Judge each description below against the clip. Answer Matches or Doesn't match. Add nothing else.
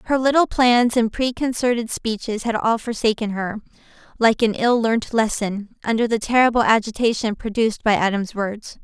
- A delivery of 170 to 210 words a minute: Doesn't match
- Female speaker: Matches